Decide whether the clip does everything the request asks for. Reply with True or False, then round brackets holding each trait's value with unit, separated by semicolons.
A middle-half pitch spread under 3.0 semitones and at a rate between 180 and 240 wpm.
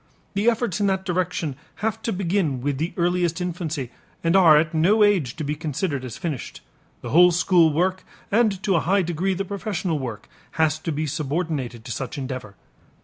False (4.3 semitones; 190 wpm)